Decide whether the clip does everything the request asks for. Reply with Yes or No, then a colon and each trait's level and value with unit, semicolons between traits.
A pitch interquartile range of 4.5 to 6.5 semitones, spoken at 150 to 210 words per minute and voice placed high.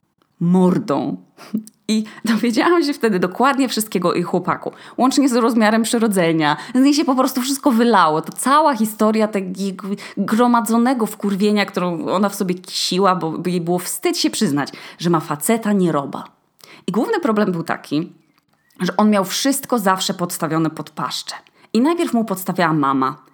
Yes: average, 5.1 semitones; average, 155 wpm; high, 200 Hz